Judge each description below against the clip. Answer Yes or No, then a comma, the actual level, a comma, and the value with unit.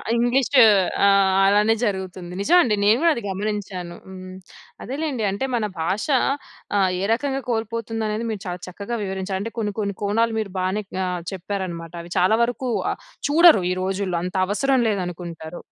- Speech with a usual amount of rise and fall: Yes, average, 3.7 semitones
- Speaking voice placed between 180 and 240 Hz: Yes, high, 205 Hz